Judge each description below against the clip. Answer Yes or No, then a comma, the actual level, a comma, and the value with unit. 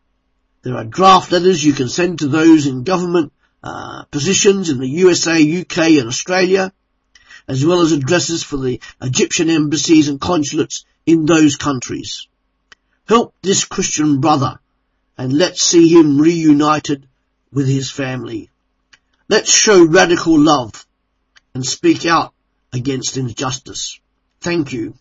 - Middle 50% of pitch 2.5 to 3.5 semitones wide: No, average, 4.8 semitones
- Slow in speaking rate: Yes, slow, 130 wpm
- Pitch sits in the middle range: Yes, medium, 155 Hz